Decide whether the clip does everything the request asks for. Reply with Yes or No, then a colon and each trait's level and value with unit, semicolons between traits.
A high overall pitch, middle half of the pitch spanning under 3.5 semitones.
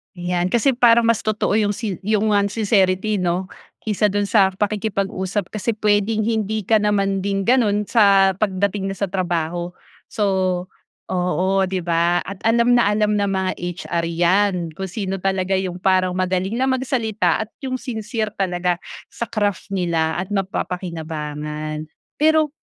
Yes: high, 195 Hz; average, 3.0 semitones